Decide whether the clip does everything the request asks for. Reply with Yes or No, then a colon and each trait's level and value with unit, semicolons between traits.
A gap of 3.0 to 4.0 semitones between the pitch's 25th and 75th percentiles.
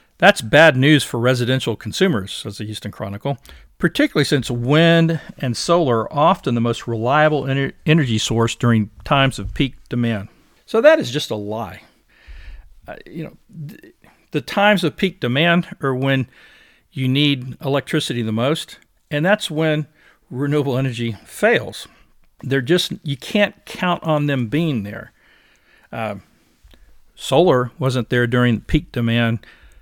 No: average, 5.2 semitones